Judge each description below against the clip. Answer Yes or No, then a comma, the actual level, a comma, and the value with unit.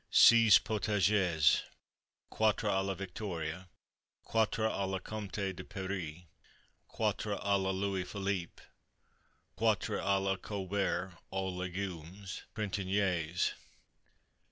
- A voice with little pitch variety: Yes, narrow, 1.9 semitones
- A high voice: No, very low, 95 Hz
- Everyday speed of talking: No, slow, 100 wpm